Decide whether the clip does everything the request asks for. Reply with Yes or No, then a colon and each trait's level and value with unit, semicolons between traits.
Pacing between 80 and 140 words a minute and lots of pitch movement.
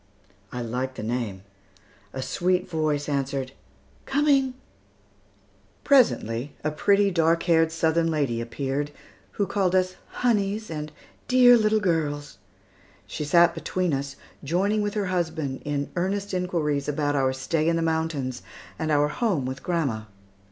No: slow, 135 wpm; average, 5.0 semitones